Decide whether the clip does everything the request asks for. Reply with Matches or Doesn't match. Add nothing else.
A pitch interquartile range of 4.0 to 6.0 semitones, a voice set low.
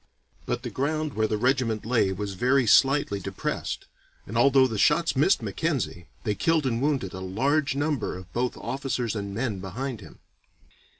Matches